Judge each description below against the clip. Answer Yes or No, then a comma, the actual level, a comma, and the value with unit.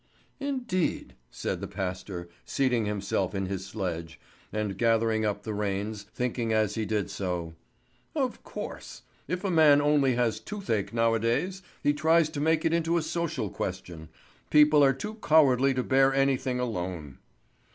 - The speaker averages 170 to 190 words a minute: No, average, 150 wpm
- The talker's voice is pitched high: No, low, 115 Hz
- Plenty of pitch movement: Yes, wide, 7.0 semitones